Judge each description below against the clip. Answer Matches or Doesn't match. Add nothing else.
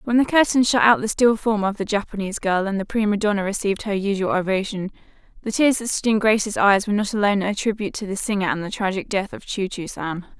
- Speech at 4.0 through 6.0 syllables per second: Doesn't match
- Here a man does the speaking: Doesn't match